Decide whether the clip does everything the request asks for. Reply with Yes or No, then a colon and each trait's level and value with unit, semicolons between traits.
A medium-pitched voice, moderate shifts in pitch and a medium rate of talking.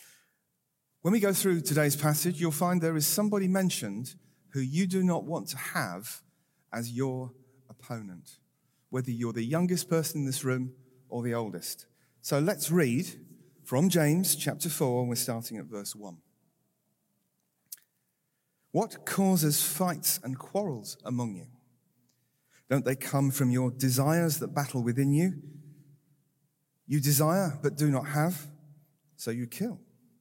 Yes: medium, 145 Hz; average, 4.5 semitones; average, 145 wpm